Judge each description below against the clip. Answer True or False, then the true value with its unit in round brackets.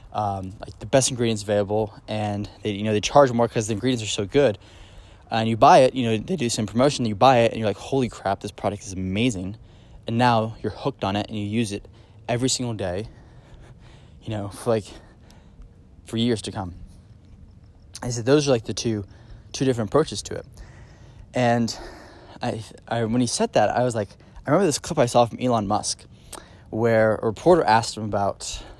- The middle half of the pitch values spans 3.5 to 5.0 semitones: False (2.9 semitones)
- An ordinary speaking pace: False (210 wpm)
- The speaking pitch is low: True (110 Hz)